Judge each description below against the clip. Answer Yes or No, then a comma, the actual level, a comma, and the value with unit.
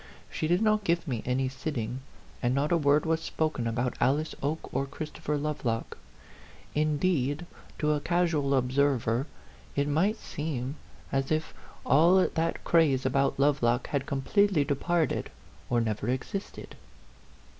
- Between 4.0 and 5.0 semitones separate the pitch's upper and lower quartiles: No, average, 3.5 semitones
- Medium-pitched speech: Yes, medium, 145 Hz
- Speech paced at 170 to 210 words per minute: No, average, 155 wpm